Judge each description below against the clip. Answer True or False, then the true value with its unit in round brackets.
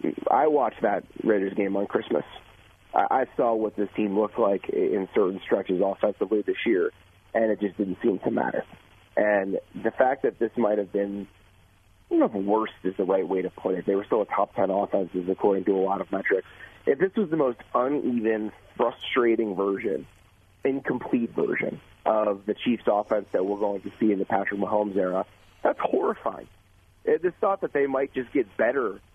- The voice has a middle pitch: False (105 Hz)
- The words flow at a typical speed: True (190 wpm)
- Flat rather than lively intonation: False (4.9 semitones)